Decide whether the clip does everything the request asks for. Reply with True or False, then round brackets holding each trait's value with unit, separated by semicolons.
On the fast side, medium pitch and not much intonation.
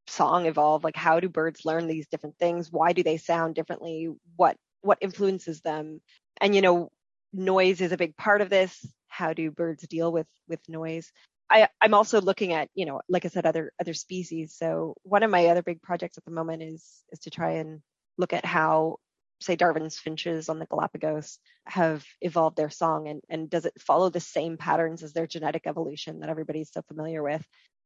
True (210 wpm; 165 Hz; 1.9 semitones)